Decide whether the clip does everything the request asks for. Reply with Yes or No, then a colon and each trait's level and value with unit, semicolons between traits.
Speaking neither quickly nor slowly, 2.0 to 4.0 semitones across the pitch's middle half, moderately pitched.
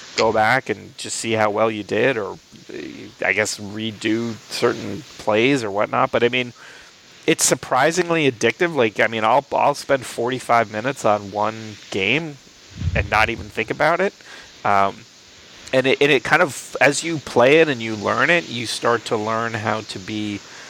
No: average, 180 wpm; average, 3.7 semitones; low, 115 Hz